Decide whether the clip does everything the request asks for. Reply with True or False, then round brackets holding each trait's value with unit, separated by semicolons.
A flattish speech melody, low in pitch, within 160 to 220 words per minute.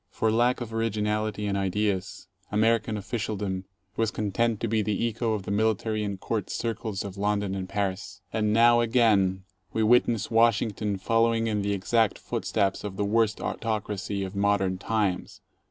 True (2.2 semitones; 105 Hz; 170 wpm)